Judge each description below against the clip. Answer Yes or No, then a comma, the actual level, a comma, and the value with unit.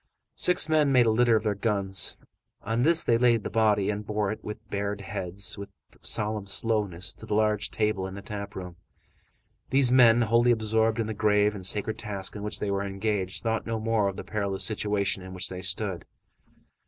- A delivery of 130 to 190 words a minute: No, fast, 205 wpm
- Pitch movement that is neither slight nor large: No, narrow, 2.2 semitones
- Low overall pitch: Yes, low, 105 Hz